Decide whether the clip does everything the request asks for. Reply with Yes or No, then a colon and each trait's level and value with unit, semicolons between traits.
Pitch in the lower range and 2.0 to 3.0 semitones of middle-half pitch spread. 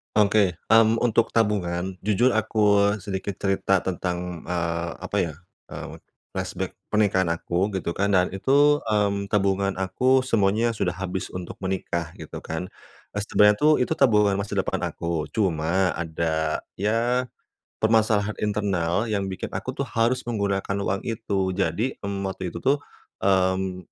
Yes: low, 100 Hz; average, 2.7 semitones